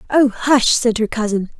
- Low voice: No, high, 235 Hz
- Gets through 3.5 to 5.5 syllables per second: Yes, 4.6 syllables/s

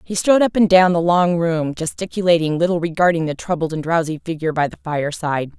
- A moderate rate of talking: Yes, average, 195 wpm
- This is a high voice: No, medium, 170 Hz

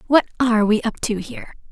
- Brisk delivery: Yes, fast, 210 wpm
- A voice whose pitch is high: Yes, high, 225 Hz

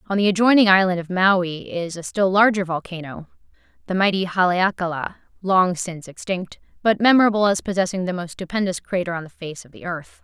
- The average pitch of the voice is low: No, medium, 185 Hz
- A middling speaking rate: Yes, average, 180 wpm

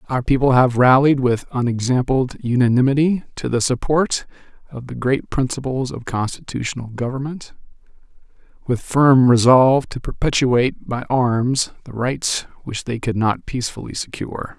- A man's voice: Yes, male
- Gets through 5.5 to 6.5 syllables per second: No, 4.9 syllables/s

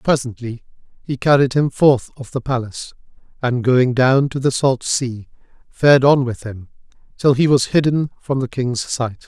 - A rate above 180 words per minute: No, average, 175 wpm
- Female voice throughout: No, male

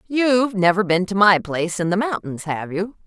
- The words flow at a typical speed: No, fast, 215 wpm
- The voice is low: No, high, 195 Hz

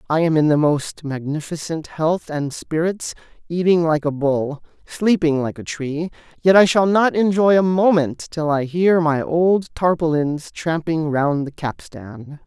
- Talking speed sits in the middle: Yes, average, 165 wpm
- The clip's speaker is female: No, male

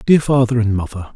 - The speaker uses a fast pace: Yes, fast, 210 wpm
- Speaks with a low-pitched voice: Yes, low, 115 Hz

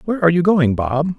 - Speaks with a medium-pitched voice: Yes, medium, 165 Hz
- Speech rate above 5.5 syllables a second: Yes, 6.6 syllables/s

